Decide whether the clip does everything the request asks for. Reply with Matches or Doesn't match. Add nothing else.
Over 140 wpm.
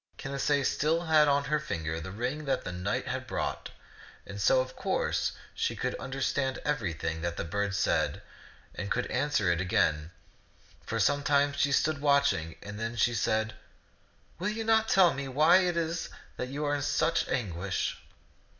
Matches